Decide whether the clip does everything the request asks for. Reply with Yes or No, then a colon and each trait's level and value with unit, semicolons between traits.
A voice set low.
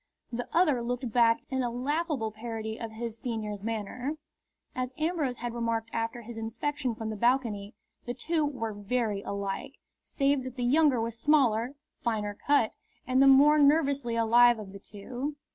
No: high, 240 Hz